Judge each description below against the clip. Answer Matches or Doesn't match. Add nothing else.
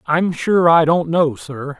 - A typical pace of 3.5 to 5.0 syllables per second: Matches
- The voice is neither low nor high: Matches